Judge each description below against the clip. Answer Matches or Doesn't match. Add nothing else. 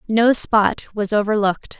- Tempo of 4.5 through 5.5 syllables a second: Matches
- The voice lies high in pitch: Matches